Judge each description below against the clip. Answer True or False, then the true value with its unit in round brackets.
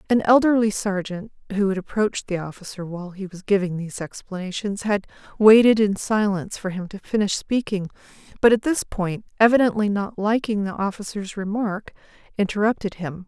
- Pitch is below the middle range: False (200 Hz)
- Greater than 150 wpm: True (160 wpm)